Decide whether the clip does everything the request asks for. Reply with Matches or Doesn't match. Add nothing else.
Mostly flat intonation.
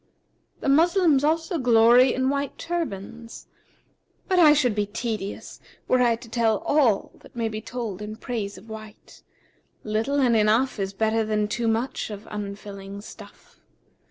Doesn't match